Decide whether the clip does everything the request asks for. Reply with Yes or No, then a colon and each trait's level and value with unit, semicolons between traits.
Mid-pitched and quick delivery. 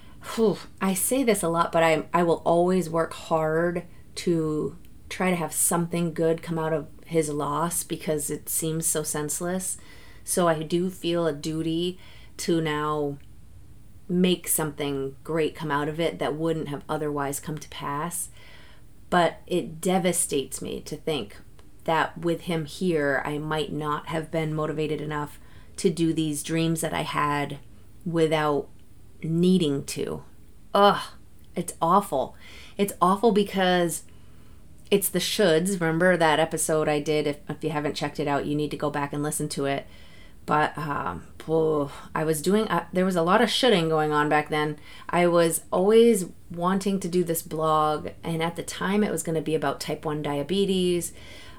No: medium, 160 Hz; average, 165 wpm